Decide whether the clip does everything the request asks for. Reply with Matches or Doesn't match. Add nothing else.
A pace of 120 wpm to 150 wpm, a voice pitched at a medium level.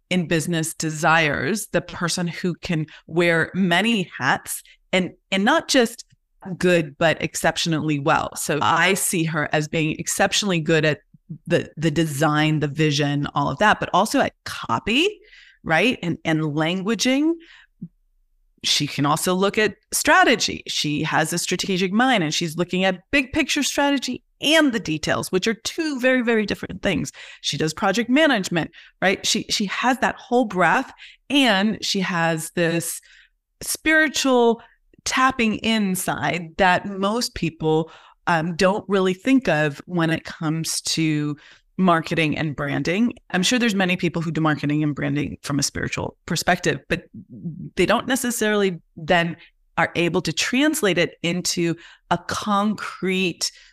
Matches